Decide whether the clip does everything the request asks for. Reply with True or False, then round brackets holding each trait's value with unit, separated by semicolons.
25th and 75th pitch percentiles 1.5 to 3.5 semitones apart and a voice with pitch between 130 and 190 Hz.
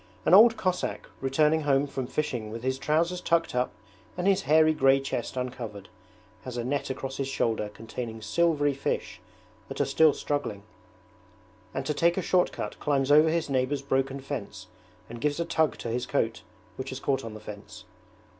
False (3.9 semitones; 135 Hz)